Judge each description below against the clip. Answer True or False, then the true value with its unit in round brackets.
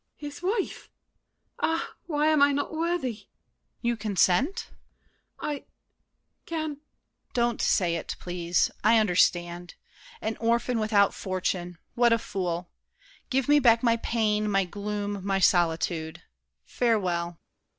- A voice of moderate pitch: False (215 Hz)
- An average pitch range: False (5.9 semitones)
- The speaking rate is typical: False (120 wpm)